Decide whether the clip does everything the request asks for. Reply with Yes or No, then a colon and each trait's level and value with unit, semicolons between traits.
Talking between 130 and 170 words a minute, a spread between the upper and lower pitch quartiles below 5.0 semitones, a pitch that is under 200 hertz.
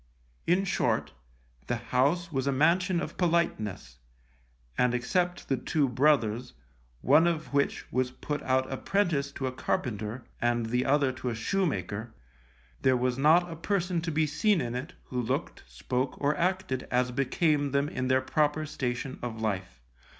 Yes: average, 160 wpm; average, 4.5 semitones; low, 135 Hz